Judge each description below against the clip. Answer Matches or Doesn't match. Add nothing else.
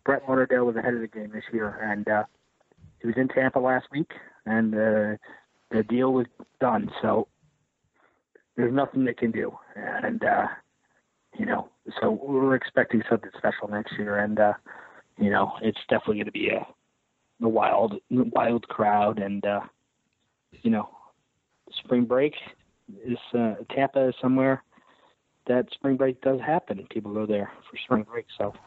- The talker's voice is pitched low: Matches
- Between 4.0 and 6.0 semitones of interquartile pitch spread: Doesn't match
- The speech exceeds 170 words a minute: Doesn't match